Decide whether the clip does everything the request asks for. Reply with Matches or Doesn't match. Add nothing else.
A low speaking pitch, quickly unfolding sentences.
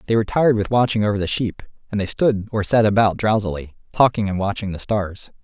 Matches